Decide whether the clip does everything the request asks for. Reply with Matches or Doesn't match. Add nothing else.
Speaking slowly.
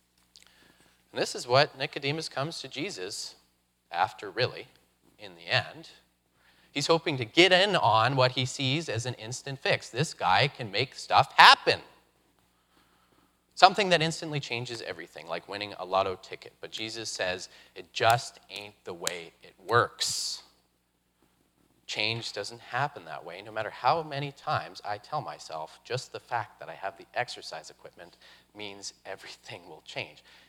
Doesn't match